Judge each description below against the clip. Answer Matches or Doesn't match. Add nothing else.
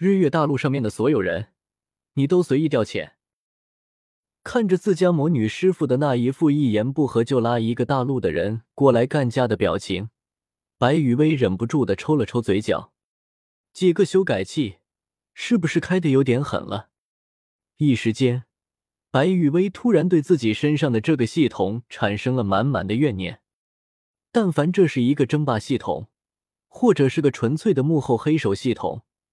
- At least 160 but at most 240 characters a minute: Doesn't match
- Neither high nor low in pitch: Doesn't match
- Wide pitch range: Matches